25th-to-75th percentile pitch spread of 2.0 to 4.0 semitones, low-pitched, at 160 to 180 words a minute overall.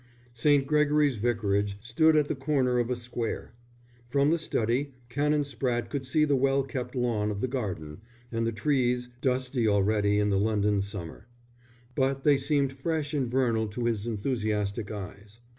No: average, 4.5 semitones; low, 125 Hz; average, 165 wpm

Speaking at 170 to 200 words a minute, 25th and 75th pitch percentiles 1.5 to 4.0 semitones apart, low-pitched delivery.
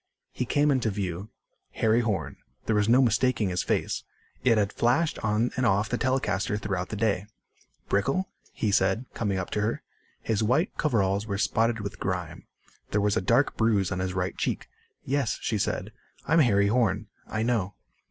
Yes: average, 180 wpm; average, 3.4 semitones; low, 105 Hz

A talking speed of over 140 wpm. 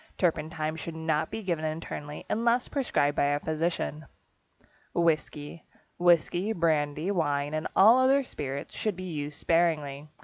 No: slow, 135 wpm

